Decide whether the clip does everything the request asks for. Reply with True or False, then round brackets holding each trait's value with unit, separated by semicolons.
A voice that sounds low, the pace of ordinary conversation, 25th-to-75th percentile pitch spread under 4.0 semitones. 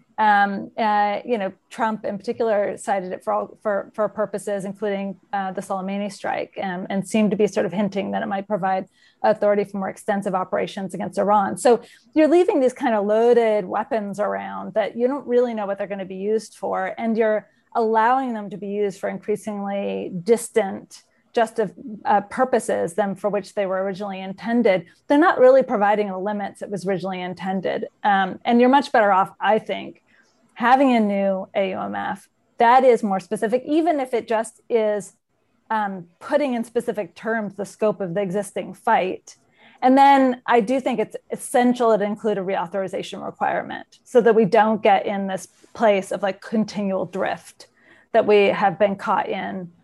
False (210 Hz; 185 wpm; 2.8 semitones)